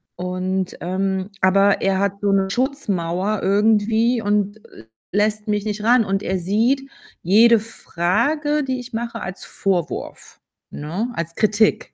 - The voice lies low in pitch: No, high, 205 Hz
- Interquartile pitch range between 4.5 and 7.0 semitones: No, average, 3.2 semitones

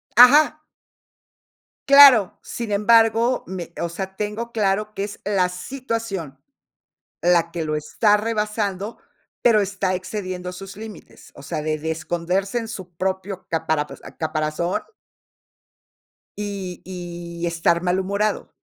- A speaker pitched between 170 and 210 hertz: Yes, high, 190 Hz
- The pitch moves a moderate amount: Yes, average, 3.7 semitones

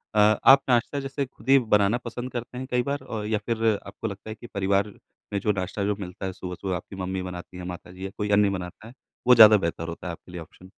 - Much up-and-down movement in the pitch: No, average, 4.2 semitones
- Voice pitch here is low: Yes, low, 105 Hz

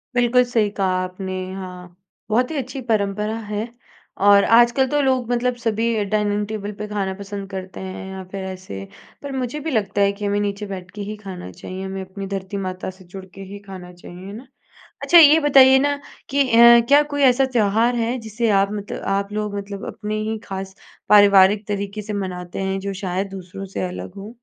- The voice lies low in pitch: No, high, 205 Hz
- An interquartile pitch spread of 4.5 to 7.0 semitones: No, average, 3.4 semitones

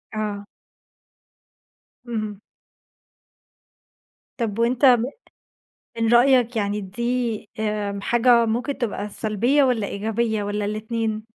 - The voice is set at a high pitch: Yes, high, 220 Hz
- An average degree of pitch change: No, narrow, 2.3 semitones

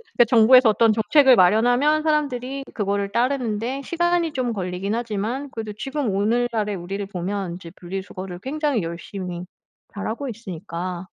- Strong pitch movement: No, average, 5.0 semitones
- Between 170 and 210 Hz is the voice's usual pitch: No, high, 220 Hz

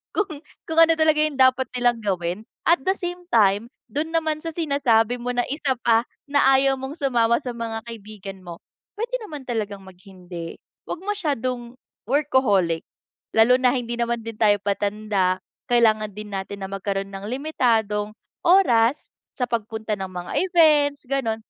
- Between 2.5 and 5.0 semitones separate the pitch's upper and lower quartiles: No, wide, 5.4 semitones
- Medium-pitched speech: No, high, 235 Hz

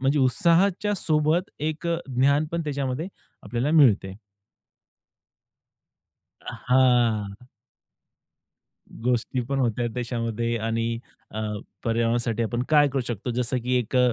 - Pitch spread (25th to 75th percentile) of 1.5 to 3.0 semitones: No, average, 3.9 semitones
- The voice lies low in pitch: Yes, low, 125 Hz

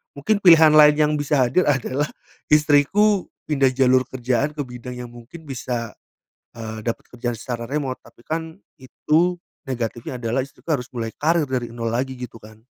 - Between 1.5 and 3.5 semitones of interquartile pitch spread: No, average, 3.9 semitones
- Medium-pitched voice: No, low, 130 Hz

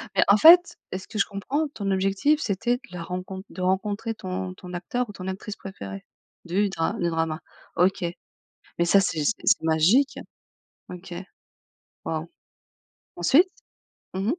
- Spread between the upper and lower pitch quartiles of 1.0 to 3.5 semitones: Yes, average, 3.1 semitones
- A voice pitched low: No, high, 190 Hz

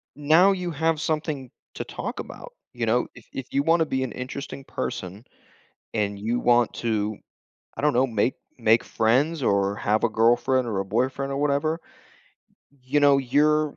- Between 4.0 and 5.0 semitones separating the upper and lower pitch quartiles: Yes, average, 4.5 semitones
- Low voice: Yes, low, 130 Hz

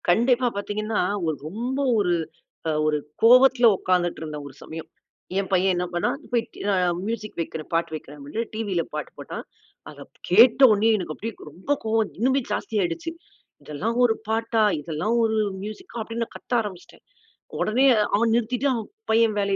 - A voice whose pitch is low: No, high, 215 Hz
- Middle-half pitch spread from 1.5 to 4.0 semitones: No, average, 4.7 semitones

